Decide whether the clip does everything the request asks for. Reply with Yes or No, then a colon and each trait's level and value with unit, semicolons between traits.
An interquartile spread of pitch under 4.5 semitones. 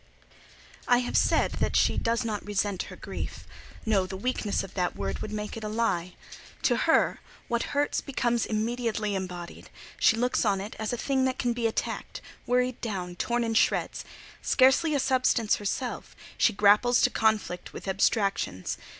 Yes: average, 3.5 semitones